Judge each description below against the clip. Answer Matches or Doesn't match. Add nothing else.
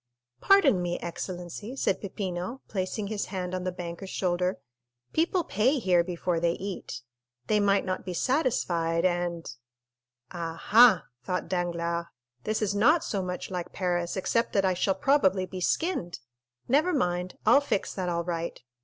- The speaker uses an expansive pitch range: Doesn't match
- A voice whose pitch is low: Doesn't match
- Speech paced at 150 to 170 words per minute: Matches